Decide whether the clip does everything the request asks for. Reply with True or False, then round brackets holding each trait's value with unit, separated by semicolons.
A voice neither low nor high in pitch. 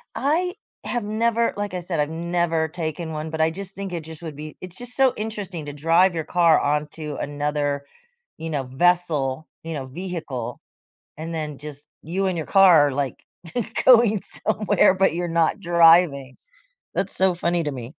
True (165 Hz)